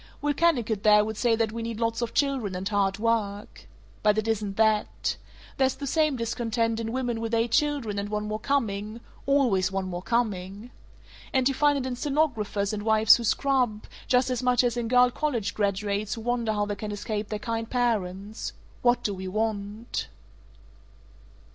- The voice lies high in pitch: Yes, high, 225 Hz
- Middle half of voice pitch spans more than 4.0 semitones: No, average, 3.0 semitones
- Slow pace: No, average, 185 wpm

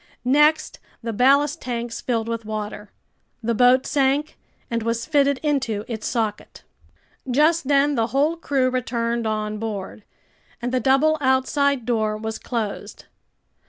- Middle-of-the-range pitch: No, high, 245 Hz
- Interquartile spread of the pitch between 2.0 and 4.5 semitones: Yes, average, 3.9 semitones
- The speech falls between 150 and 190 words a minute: No, slow, 135 wpm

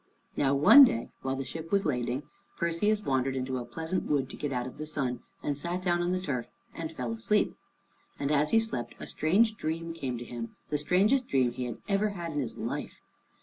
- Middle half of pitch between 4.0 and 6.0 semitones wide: Yes, wide, 5.5 semitones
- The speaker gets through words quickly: Yes, fast, 220 wpm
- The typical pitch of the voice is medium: Yes, medium, 150 Hz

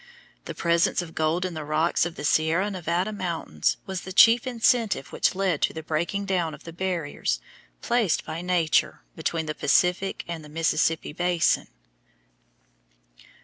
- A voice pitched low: No, medium, 170 Hz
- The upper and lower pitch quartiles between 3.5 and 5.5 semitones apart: No, average, 2.9 semitones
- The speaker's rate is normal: Yes, average, 155 wpm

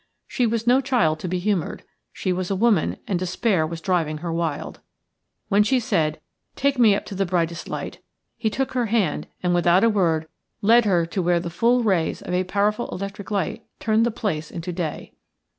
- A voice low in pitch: No, high, 190 Hz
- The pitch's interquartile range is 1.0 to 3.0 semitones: No, average, 4.5 semitones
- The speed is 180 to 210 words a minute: Yes, average, 200 wpm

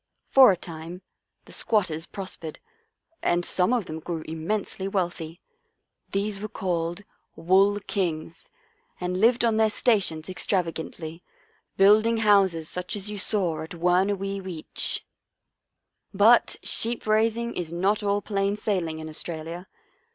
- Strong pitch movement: No, average, 3.8 semitones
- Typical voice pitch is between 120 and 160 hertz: No, high, 190 Hz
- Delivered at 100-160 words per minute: Yes, average, 145 wpm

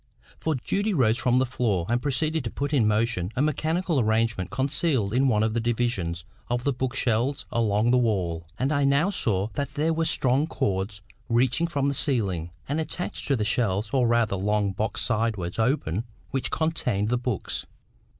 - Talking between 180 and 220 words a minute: Yes, average, 185 wpm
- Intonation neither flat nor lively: Yes, average, 4.8 semitones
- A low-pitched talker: Yes, low, 120 Hz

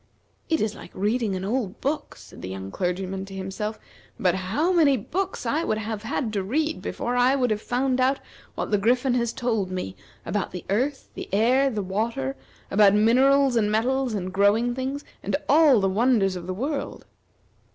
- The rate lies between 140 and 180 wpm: No, average, 190 wpm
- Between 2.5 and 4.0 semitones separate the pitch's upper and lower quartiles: No, average, 5.2 semitones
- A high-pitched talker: Yes, high, 220 Hz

